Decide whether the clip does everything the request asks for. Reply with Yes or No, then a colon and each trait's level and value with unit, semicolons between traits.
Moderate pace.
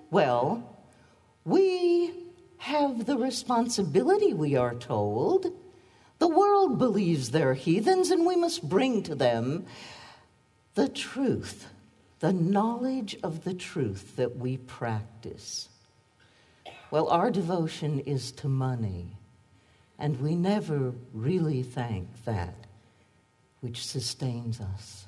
No: slow, 105 wpm